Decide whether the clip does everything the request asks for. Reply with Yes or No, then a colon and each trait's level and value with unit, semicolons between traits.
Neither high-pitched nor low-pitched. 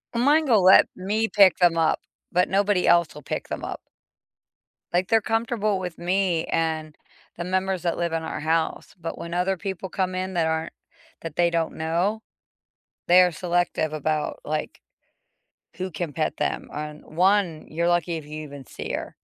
Yes: medium, 175 Hz